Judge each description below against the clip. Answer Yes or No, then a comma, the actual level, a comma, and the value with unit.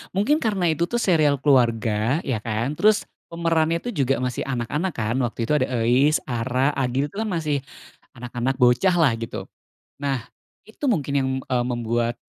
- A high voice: No, low, 135 Hz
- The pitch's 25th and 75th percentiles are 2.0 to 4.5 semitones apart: No, wide, 5.4 semitones